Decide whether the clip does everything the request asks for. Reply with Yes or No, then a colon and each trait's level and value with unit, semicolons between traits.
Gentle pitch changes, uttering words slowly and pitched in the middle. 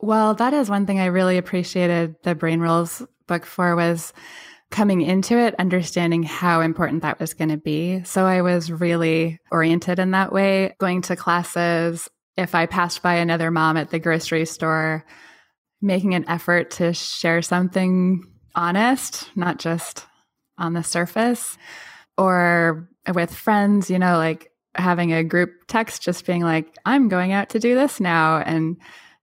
No: narrow, 2.0 semitones; average, 160 wpm; medium, 175 Hz